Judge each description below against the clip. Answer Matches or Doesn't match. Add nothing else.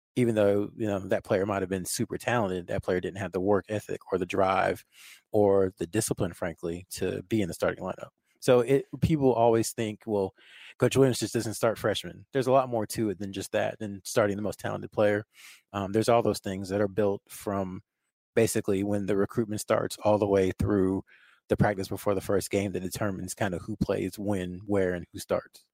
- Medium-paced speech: Doesn't match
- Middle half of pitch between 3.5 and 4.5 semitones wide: Doesn't match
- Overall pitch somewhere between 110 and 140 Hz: Doesn't match